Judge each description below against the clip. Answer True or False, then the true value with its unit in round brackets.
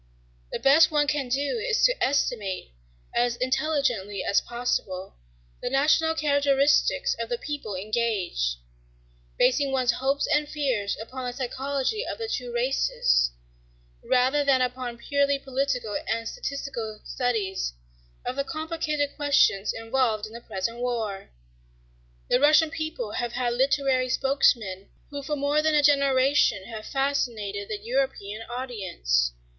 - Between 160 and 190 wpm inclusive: False (135 wpm)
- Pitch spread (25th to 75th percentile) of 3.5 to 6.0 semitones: True (4.1 semitones)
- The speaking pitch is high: True (255 Hz)